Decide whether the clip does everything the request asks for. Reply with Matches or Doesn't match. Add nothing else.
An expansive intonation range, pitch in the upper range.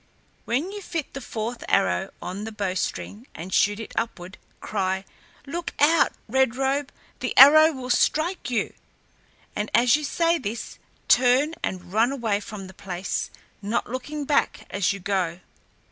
Matches